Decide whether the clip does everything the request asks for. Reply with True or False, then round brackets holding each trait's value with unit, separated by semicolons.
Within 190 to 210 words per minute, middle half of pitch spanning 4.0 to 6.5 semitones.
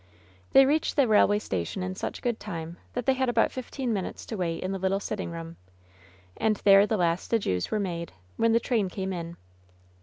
True (205 wpm; 4.8 semitones)